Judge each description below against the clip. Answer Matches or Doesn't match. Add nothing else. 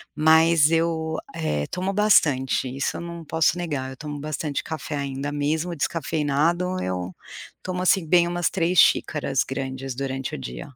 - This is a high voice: Doesn't match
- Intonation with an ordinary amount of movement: Matches